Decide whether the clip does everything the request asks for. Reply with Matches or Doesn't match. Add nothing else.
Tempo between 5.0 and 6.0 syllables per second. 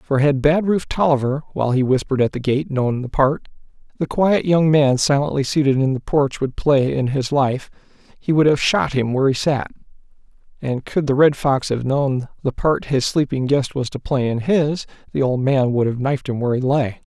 Matches